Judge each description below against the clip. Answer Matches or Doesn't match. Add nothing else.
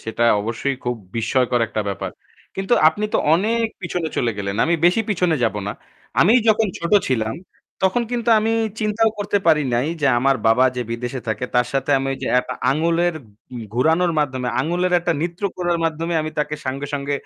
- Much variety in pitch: Matches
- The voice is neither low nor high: Matches